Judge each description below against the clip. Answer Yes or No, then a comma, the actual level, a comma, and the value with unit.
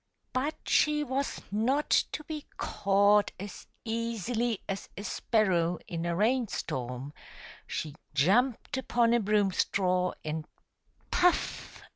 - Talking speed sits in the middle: No, slow, 125 wpm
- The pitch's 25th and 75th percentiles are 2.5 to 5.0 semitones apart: No, wide, 5.5 semitones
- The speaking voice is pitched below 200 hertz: No, high, 210 Hz